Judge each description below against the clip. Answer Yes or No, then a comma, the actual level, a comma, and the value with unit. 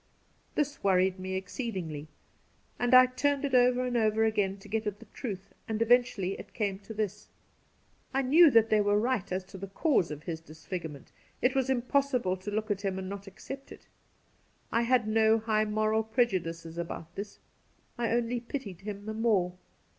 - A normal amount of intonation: Yes, average, 4.2 semitones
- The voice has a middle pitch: No, high, 215 Hz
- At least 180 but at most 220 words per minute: Yes, average, 185 wpm